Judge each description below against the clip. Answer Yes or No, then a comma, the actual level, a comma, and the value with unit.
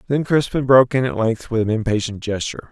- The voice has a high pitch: No, low, 120 Hz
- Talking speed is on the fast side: Yes, fast, 220 wpm